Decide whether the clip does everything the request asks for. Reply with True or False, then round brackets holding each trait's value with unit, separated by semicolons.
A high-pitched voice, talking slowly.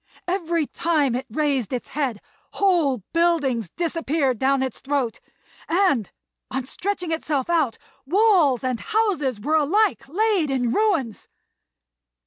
True (295 Hz; 120 wpm)